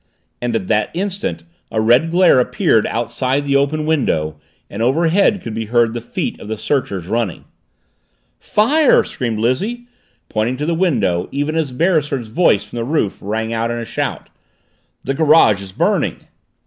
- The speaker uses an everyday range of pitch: No, wide, 6.4 semitones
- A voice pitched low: Yes, low, 125 Hz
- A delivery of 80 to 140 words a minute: No, average, 165 wpm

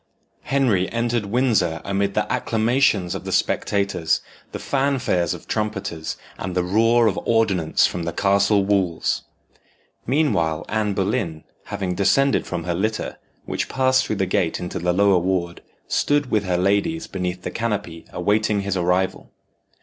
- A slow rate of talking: No, average, 150 wpm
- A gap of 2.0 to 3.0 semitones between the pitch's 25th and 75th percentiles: No, average, 4.0 semitones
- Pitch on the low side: Yes, low, 100 Hz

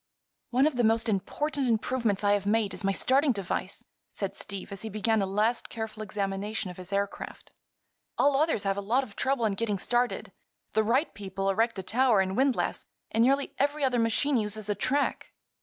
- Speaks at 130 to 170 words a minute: No, average, 195 wpm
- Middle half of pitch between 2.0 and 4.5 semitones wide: Yes, average, 4.1 semitones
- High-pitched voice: Yes, high, 220 Hz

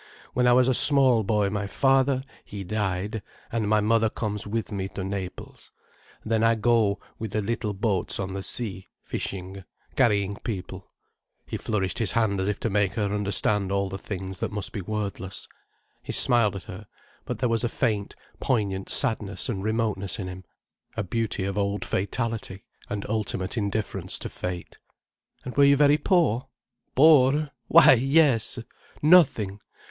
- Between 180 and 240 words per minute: No, average, 160 wpm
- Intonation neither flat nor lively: Yes, average, 3.1 semitones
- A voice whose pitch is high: No, low, 105 Hz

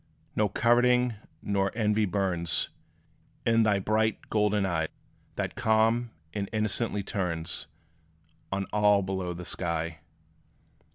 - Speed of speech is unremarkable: No, slow, 110 wpm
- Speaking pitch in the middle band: No, low, 105 Hz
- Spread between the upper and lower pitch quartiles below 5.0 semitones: Yes, average, 2.8 semitones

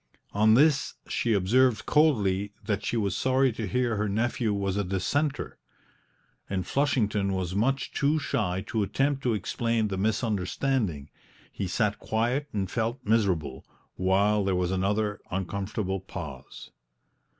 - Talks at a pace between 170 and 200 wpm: No, average, 140 wpm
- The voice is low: Yes, low, 105 Hz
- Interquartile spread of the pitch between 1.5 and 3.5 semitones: No, average, 4.0 semitones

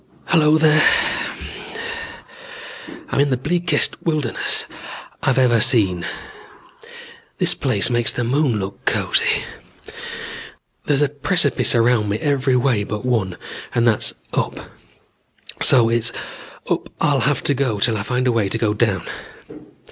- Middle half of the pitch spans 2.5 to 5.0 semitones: Yes, average, 4.2 semitones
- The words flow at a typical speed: No, slow, 130 wpm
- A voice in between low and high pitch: No, low, 120 Hz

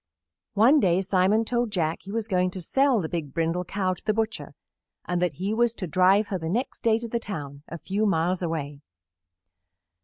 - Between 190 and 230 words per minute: Yes, fast, 205 wpm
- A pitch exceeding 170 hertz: Yes, high, 190 Hz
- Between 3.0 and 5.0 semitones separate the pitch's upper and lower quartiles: Yes, average, 4.4 semitones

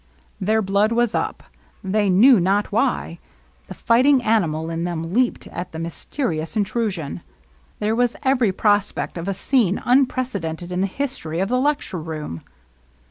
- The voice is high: Yes, high, 200 Hz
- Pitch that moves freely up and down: Yes, wide, 5.8 semitones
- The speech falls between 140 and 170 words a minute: Yes, average, 155 wpm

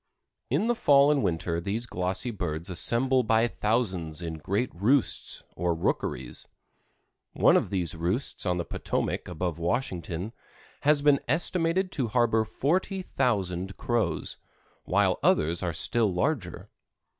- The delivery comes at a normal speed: No, slow, 130 wpm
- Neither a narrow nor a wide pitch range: No, wide, 7.1 semitones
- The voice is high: No, low, 105 Hz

